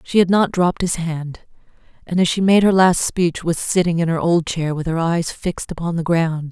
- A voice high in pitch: No, medium, 170 Hz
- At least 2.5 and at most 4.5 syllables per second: No, 5.1 syllables/s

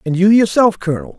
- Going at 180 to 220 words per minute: Yes, fast, 205 wpm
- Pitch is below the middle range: No, high, 190 Hz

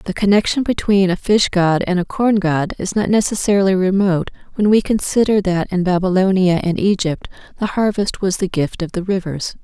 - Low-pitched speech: No, high, 190 Hz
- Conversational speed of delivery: Yes, average, 185 wpm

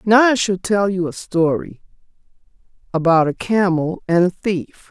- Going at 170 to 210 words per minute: No, average, 160 wpm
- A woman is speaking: Yes, female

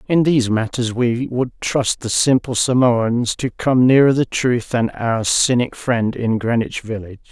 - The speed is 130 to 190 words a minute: Yes, average, 170 wpm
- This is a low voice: Yes, low, 120 Hz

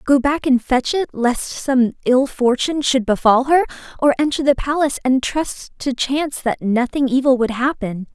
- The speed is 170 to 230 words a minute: Yes, average, 185 wpm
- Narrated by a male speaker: No, female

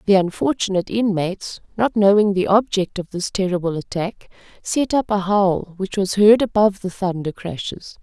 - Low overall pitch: No, high, 195 Hz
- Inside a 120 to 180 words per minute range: Yes, average, 165 wpm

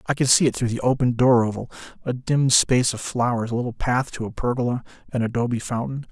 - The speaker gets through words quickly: Yes, fast, 215 wpm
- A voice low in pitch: Yes, low, 125 Hz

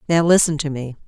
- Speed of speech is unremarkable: No, fast, 225 wpm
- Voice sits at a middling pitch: Yes, medium, 155 Hz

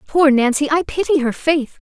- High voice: Yes, very high, 290 Hz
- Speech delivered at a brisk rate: No, average, 190 wpm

